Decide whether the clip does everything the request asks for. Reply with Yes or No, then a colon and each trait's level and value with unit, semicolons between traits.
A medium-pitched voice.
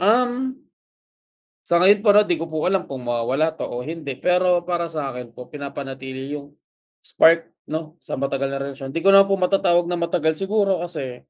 Yes: medium, 165 Hz